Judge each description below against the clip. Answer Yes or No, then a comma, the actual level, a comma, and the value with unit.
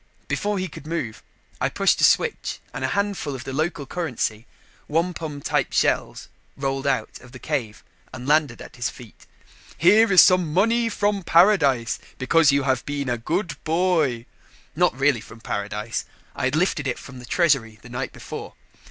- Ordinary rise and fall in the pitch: No, wide, 5.8 semitones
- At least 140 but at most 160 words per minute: No, average, 175 wpm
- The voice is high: No, medium, 145 Hz